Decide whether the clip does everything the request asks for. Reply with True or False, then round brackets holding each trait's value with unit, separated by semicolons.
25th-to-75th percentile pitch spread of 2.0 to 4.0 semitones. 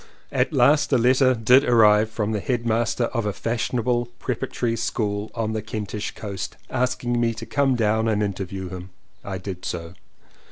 True (2.8 semitones)